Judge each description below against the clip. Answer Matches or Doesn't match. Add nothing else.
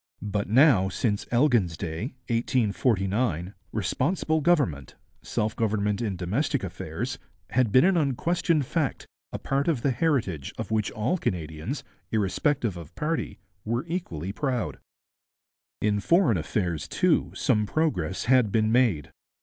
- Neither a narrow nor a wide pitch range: Doesn't match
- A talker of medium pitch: Doesn't match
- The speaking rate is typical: Doesn't match